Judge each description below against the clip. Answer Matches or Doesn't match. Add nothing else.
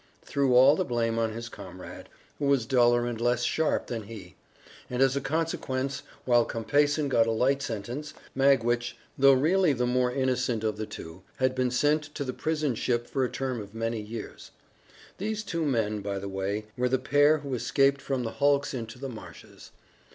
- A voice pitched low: Matches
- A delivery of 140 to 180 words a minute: Doesn't match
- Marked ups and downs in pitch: Doesn't match